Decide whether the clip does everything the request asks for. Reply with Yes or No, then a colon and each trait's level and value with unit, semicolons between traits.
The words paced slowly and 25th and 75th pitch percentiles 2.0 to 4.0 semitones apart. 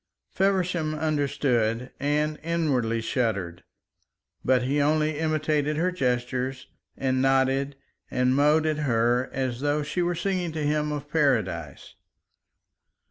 Yes: slow, 120 wpm; average, 3.5 semitones